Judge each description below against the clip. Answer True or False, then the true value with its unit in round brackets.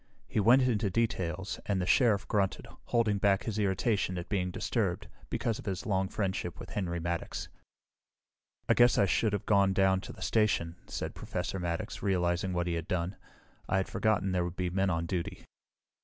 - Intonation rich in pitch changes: False (2.7 semitones)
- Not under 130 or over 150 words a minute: False (185 wpm)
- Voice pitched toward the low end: True (95 Hz)